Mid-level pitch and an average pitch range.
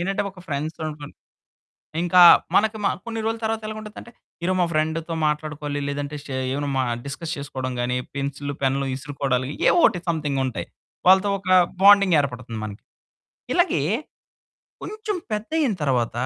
No: medium, 155 Hz; wide, 6.3 semitones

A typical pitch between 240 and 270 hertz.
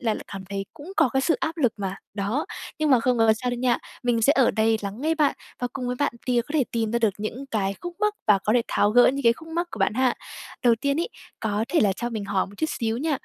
Yes: high, 245 Hz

